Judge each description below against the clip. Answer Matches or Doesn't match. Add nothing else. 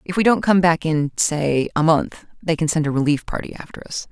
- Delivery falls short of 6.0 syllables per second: Matches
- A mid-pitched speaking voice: Matches